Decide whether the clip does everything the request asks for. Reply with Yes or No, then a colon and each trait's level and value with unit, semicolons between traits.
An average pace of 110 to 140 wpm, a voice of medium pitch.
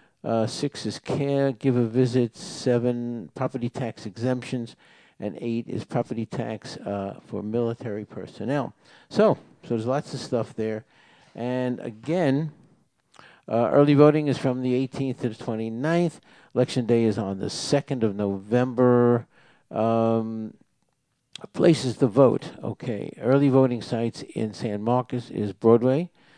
No: slow, 135 wpm; low, 125 Hz